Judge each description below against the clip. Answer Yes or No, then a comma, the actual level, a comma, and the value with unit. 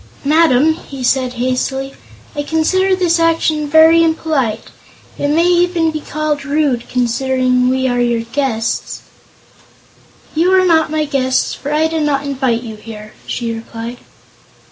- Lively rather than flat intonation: No, average, 4.3 semitones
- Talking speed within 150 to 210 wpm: No, average, 140 wpm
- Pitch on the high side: Yes, very high, 280 Hz